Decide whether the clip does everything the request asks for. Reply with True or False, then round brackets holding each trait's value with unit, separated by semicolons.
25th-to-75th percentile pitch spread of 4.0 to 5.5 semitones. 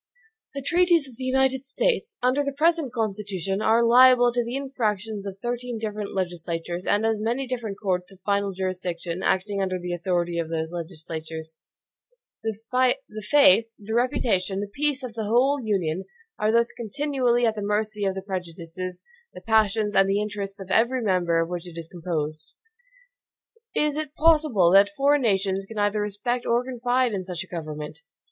True (5.1 semitones)